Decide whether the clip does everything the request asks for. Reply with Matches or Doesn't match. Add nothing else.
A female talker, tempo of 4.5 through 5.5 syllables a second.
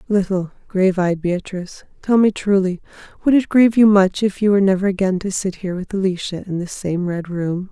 Doesn't match